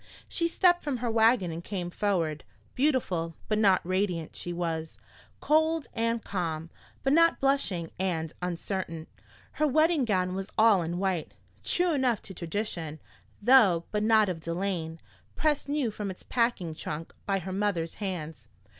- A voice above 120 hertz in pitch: Yes, high, 190 Hz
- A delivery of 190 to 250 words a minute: No, average, 150 wpm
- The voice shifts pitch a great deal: Yes, wide, 6.3 semitones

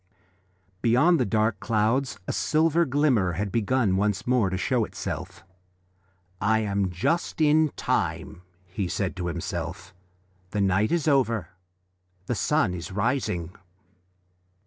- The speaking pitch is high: No, low, 105 Hz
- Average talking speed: No, slow, 125 wpm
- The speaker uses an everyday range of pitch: No, wide, 5.7 semitones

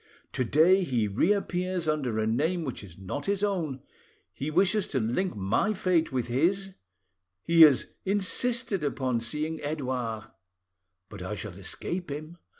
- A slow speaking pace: No, average, 150 wpm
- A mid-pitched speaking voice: Yes, medium, 155 Hz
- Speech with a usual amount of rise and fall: No, wide, 7.4 semitones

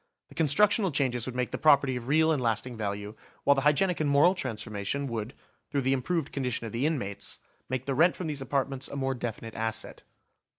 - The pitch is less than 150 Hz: Yes, low, 135 Hz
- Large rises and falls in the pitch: No, average, 4.0 semitones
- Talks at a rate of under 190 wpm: No, fast, 205 wpm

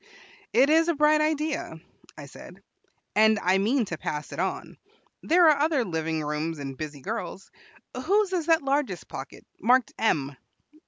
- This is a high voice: Yes, very high, 250 Hz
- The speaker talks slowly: No, average, 160 wpm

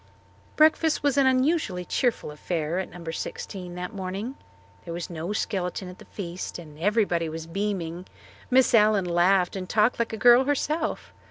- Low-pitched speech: No, high, 190 Hz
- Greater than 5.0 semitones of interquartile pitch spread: Yes, wide, 5.5 semitones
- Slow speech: No, average, 165 wpm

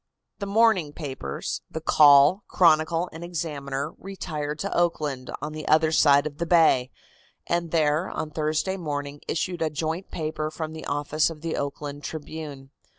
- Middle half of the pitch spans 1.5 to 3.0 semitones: Yes, narrow, 2.4 semitones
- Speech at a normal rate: Yes, average, 155 wpm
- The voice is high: No, medium, 155 Hz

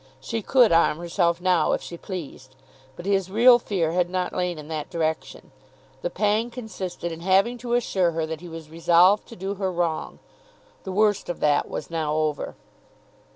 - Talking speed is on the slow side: No, average, 185 wpm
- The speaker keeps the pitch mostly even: No, average, 3.7 semitones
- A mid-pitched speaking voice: Yes, medium, 180 Hz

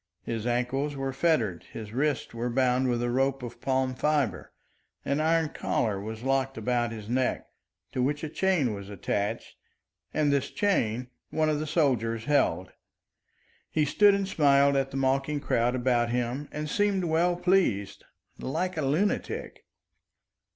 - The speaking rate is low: No, average, 155 wpm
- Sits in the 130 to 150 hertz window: Yes, low, 135 Hz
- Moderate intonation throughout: Yes, average, 4.1 semitones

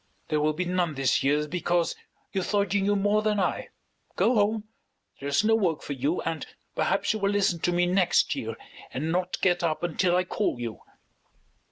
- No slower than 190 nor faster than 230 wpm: Yes, average, 200 wpm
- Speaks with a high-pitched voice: No, medium, 175 Hz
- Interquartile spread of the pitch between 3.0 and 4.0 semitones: No, average, 4.5 semitones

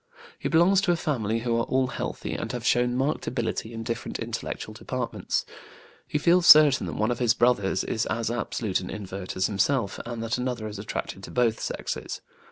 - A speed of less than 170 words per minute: No, average, 195 wpm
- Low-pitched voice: Yes, low, 120 Hz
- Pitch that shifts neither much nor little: Yes, average, 3.3 semitones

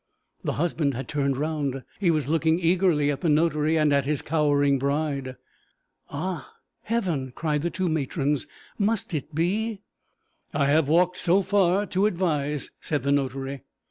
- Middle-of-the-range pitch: Yes, medium, 155 Hz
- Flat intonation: No, average, 3.6 semitones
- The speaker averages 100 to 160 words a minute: Yes, average, 155 wpm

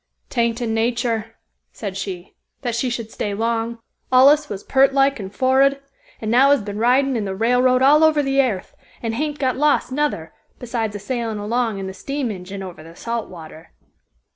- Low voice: No, high, 235 Hz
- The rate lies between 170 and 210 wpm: Yes, average, 190 wpm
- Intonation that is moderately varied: Yes, average, 4.5 semitones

